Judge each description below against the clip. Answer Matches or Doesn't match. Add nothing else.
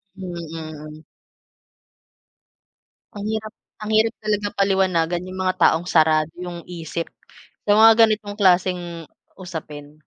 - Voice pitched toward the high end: Doesn't match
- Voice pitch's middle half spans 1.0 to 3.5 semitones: Doesn't match